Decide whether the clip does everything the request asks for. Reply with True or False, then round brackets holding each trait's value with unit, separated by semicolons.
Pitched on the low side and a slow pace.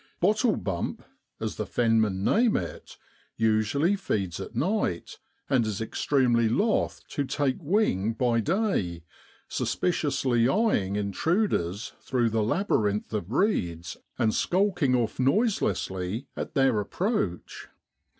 True (120 Hz; 120 wpm)